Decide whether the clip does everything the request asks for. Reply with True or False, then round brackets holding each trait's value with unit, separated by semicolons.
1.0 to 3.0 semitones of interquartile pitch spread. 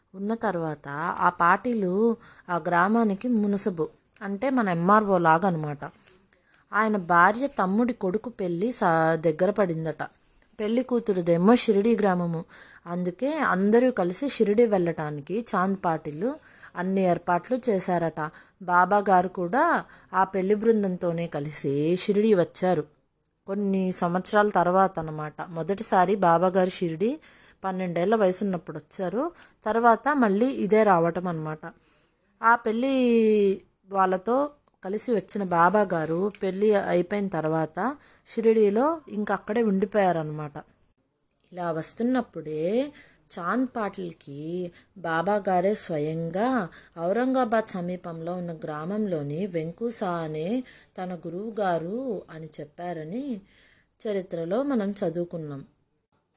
False (4.3 semitones)